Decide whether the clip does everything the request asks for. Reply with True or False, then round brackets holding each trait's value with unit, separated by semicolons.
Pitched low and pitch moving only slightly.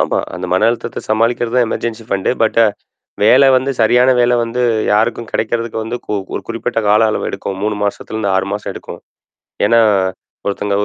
True (115 Hz; 2.3 semitones)